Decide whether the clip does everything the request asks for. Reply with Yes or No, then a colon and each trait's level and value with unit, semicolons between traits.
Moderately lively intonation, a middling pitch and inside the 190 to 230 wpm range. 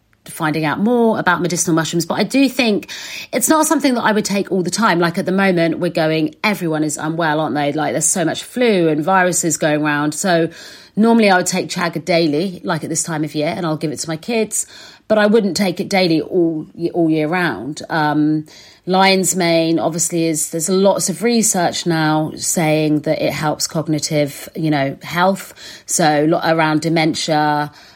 Yes: average, 3.4 semitones; medium, 170 Hz; average, 195 wpm